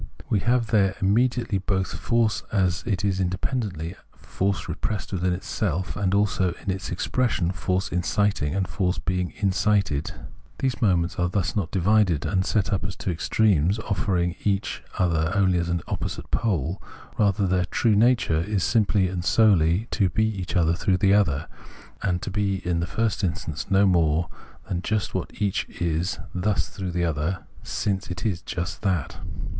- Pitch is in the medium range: No, very low, 95 Hz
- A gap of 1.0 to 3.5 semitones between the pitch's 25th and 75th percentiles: Yes, average, 2.8 semitones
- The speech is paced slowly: No, average, 160 wpm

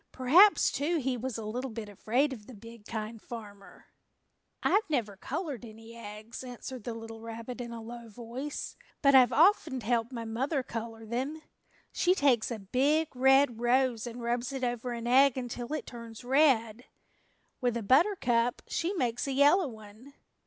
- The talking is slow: No, average, 165 wpm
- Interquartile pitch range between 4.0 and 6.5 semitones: No, average, 2.9 semitones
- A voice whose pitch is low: No, high, 240 Hz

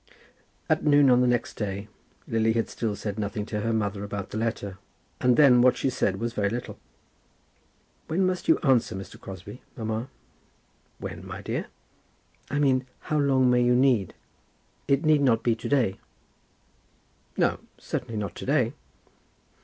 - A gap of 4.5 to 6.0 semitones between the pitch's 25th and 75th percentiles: No, average, 4.1 semitones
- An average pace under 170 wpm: Yes, average, 160 wpm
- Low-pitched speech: Yes, low, 115 Hz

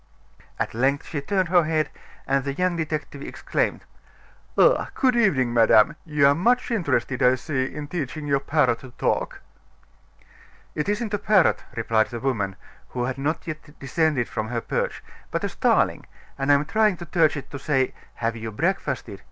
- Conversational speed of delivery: Yes, average, 175 wpm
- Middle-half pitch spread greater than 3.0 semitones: Yes, average, 4.7 semitones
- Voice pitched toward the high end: No, medium, 145 Hz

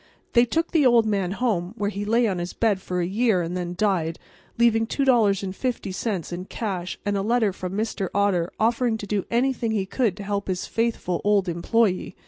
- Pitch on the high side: Yes, high, 205 Hz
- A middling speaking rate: Yes, average, 195 wpm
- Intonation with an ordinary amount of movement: Yes, average, 3.9 semitones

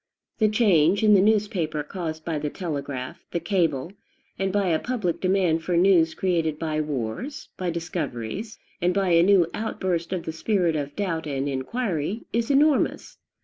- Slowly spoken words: No, average, 165 wpm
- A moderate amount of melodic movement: Yes, average, 4.2 semitones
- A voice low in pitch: No, medium, 175 Hz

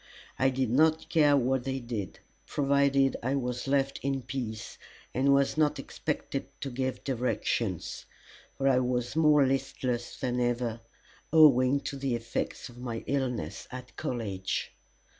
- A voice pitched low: Yes, low, 130 Hz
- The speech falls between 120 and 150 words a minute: Yes, average, 140 wpm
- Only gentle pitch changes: Yes, narrow, 2.2 semitones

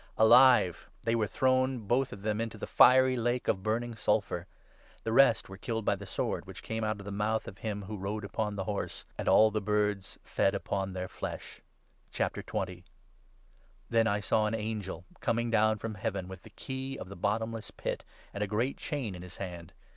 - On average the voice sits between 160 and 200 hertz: No, low, 110 Hz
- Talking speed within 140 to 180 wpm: No, average, 200 wpm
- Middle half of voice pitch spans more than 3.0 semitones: No, narrow, 2.5 semitones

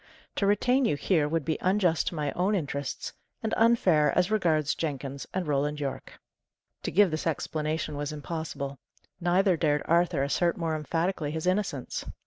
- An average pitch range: Yes, average, 3.7 semitones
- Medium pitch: Yes, medium, 160 Hz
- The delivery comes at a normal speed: Yes, average, 160 wpm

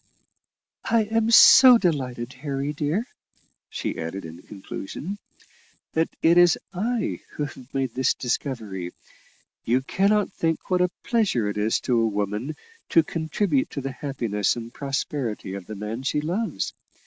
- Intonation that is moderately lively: No, wide, 7.6 semitones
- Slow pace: No, average, 150 wpm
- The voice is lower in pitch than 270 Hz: Yes, low, 135 Hz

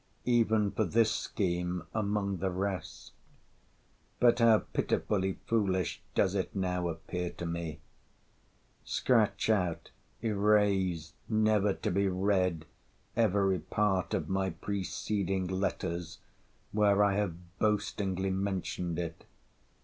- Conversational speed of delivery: No, slow, 105 wpm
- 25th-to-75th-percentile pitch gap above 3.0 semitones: No, narrow, 2.6 semitones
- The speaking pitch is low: Yes, very low, 95 Hz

